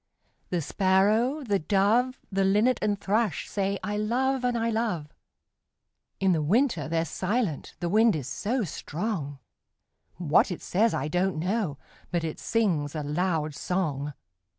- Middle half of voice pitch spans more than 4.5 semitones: Yes, wide, 5.6 semitones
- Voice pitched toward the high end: Yes, high, 195 Hz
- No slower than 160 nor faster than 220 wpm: No, average, 150 wpm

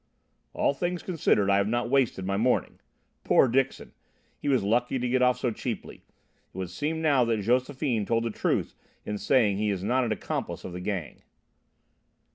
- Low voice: Yes, low, 120 Hz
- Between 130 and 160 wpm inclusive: No, average, 185 wpm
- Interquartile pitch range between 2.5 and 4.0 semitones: No, average, 4.4 semitones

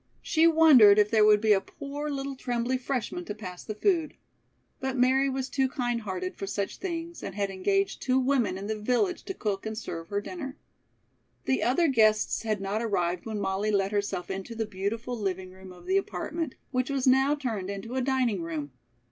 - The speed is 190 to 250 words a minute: Yes, average, 200 wpm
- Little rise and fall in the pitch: No, average, 5.1 semitones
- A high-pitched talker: Yes, high, 225 Hz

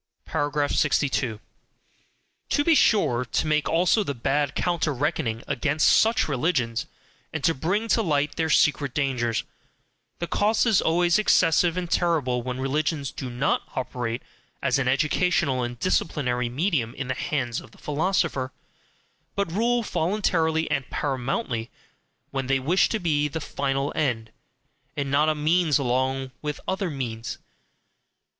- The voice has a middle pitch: Yes, medium, 145 Hz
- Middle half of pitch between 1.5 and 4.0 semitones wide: No, average, 4.5 semitones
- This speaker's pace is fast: No, average, 140 wpm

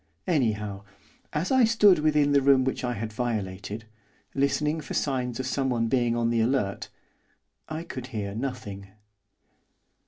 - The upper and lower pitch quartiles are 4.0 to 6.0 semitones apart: Yes, average, 4.3 semitones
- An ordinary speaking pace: Yes, average, 145 wpm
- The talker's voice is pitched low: Yes, low, 125 Hz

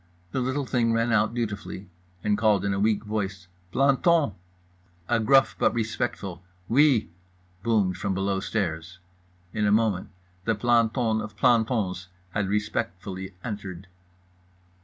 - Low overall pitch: Yes, low, 105 Hz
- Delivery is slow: Yes, slow, 130 wpm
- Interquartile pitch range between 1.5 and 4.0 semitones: Yes, average, 3.3 semitones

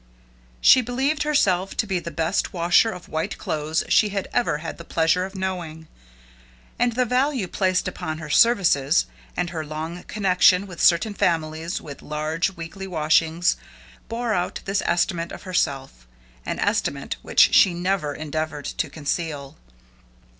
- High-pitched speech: No, medium, 175 Hz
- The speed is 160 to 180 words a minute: No, average, 150 wpm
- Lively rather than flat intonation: No, average, 3.7 semitones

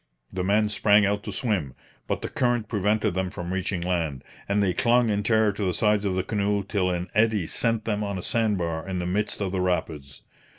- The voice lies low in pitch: Yes, low, 100 Hz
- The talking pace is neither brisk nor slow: No, fast, 225 wpm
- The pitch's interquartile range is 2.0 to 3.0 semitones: Yes, average, 2.7 semitones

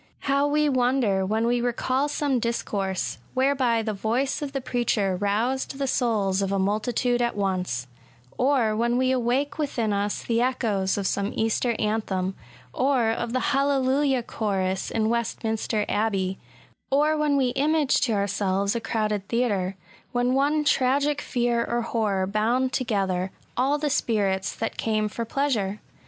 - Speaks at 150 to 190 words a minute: Yes, average, 160 wpm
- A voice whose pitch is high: Yes, high, 235 Hz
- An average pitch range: Yes, average, 4.3 semitones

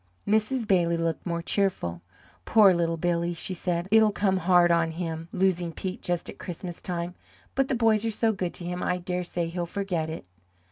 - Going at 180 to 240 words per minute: Yes, average, 195 wpm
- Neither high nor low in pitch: Yes, medium, 180 Hz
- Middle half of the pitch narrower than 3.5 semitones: Yes, narrow, 2.5 semitones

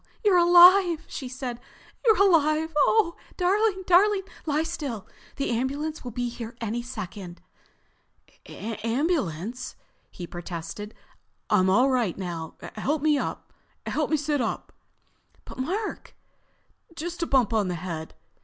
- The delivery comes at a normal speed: No, slow, 115 wpm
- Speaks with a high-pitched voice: Yes, very high, 265 Hz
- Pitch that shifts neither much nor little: No, wide, 7.9 semitones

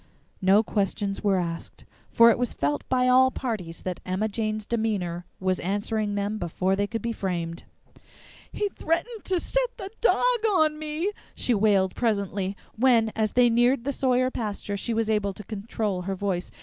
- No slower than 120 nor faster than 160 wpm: No, average, 175 wpm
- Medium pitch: No, high, 215 Hz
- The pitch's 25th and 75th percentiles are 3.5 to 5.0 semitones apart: Yes, average, 4.3 semitones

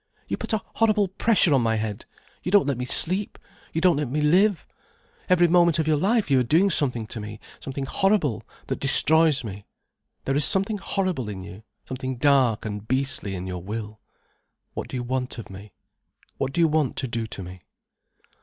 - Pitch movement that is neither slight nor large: No, wide, 7.5 semitones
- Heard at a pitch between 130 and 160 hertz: Yes, low, 135 Hz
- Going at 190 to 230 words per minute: Yes, average, 200 wpm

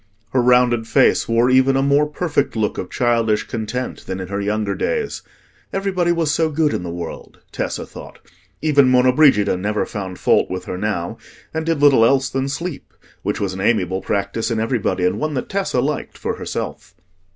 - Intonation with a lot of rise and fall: Yes, wide, 5.9 semitones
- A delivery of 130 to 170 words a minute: No, average, 190 wpm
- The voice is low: Yes, low, 125 Hz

